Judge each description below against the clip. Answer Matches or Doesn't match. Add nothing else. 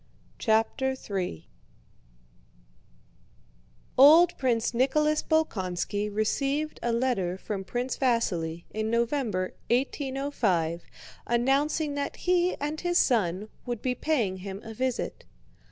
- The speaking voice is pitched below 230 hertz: Doesn't match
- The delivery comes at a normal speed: Doesn't match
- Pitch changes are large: Matches